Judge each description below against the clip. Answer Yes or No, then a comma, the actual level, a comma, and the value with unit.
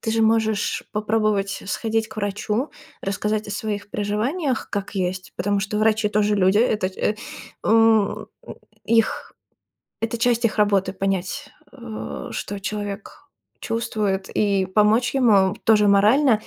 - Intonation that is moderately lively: No, narrow, 2.0 semitones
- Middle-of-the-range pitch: No, high, 210 Hz